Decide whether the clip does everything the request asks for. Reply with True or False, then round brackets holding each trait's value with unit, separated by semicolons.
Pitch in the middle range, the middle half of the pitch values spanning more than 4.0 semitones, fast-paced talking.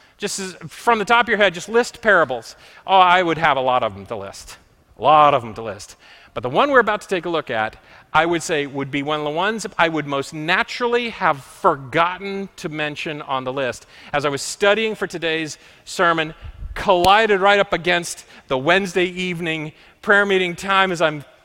True (170 Hz; 4.7 semitones; 210 wpm)